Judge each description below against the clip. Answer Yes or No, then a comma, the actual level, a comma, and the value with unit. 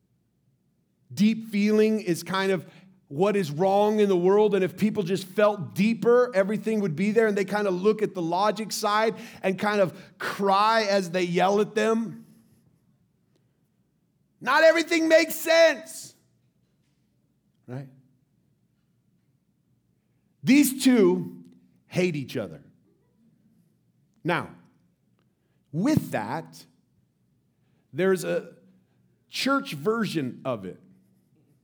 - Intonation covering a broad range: No, average, 3.7 semitones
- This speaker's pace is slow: Yes, slow, 110 wpm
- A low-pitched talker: No, high, 200 Hz